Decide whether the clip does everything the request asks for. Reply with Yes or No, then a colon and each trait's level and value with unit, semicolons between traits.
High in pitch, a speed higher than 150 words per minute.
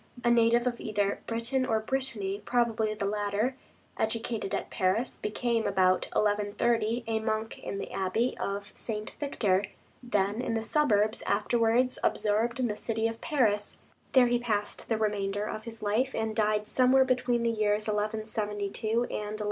Yes: high, 220 Hz; average, 160 wpm